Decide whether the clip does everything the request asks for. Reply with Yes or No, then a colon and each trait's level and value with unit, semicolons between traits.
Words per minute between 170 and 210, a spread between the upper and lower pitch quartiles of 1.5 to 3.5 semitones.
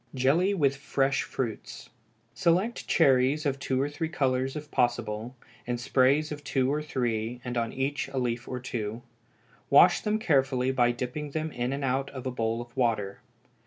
Yes: average, 175 wpm; average, 3.1 semitones